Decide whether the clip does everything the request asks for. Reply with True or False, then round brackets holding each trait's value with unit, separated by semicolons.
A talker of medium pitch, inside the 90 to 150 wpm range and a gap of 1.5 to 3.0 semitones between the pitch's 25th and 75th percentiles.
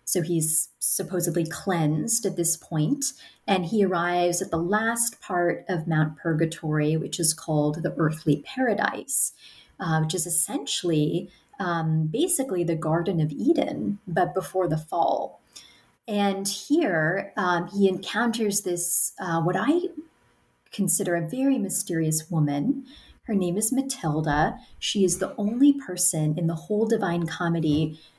False (180 Hz; 140 wpm; 4.3 semitones)